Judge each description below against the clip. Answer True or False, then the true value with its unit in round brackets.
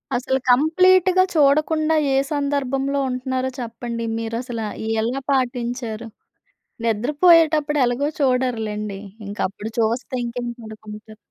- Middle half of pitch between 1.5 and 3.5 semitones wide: False (3.9 semitones)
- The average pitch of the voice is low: False (255 Hz)